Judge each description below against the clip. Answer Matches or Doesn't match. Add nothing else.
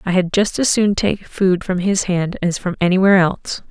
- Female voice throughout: Matches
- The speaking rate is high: Matches